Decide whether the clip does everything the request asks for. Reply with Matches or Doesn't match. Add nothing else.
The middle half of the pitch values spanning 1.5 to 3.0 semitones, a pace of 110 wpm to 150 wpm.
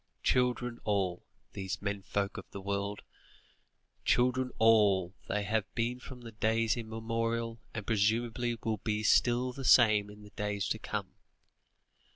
Matches